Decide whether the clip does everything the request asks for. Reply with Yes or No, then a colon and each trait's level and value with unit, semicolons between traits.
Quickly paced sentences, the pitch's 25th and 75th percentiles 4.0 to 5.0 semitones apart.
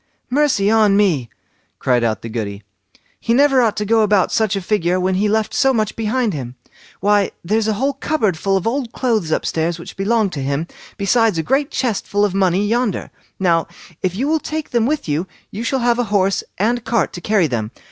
Yes: fast, 215 wpm; average, 4.7 semitones